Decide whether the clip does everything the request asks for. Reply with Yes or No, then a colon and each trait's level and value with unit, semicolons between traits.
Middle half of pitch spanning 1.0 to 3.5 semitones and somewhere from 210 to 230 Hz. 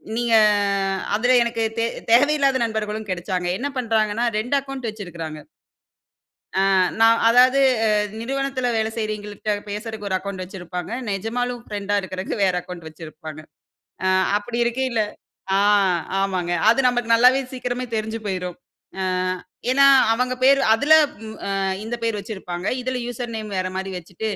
No: average, 4.2 semitones; high, 220 Hz